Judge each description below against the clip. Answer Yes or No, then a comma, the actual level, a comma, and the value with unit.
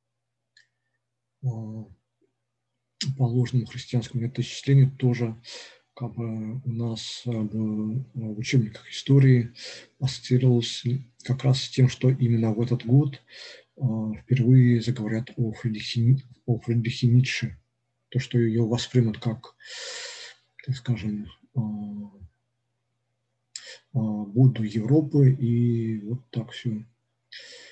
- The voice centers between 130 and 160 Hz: No, low, 120 Hz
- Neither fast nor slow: No, slow, 95 wpm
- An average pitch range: No, narrow, 1.8 semitones